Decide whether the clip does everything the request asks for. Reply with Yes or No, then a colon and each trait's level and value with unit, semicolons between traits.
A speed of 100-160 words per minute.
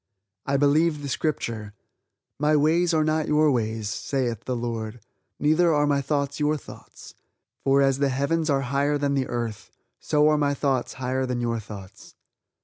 No: average, 170 wpm